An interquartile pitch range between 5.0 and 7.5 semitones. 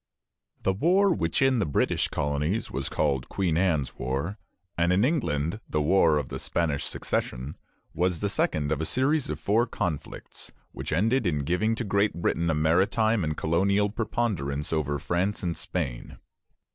Yes: wide, 5.6 semitones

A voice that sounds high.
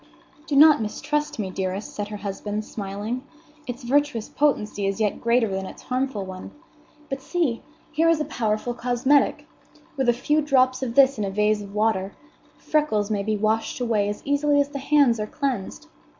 Yes: high, 235 Hz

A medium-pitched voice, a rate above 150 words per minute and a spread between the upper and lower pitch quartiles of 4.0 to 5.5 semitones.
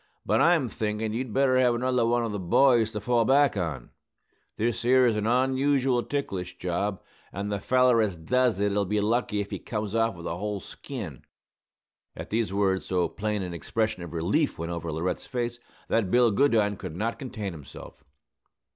No: low, 110 Hz; average, 180 wpm; average, 4.4 semitones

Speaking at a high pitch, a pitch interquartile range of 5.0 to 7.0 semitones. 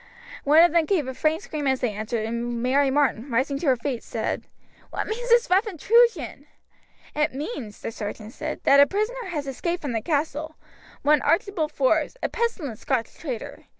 Yes: very high, 290 Hz; wide, 5.4 semitones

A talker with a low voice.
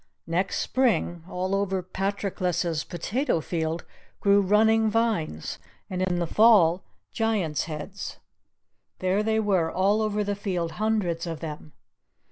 No: high, 190 Hz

